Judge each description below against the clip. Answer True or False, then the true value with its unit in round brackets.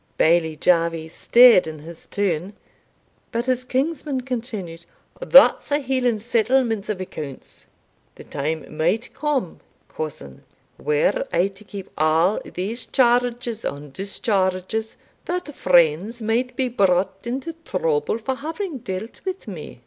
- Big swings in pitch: True (6.8 semitones)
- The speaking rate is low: True (125 wpm)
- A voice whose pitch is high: True (210 Hz)